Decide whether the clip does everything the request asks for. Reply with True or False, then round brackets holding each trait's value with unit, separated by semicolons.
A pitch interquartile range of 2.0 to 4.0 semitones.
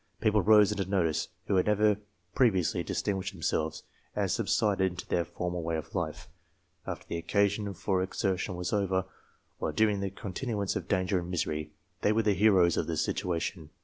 True (2.8 semitones)